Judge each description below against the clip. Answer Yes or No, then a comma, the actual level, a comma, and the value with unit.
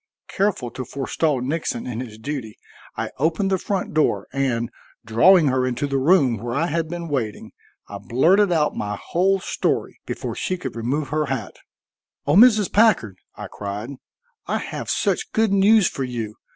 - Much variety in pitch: Yes, wide, 6.9 semitones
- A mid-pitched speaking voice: Yes, medium, 145 Hz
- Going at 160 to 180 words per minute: Yes, average, 170 wpm